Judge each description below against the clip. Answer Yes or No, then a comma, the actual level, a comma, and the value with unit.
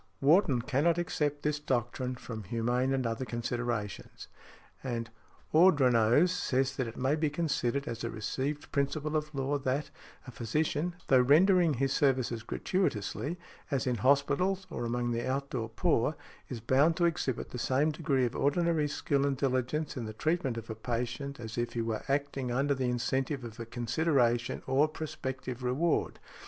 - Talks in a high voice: No, low, 135 Hz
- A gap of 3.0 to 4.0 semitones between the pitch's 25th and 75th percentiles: Yes, average, 3.7 semitones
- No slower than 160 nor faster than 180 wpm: Yes, average, 165 wpm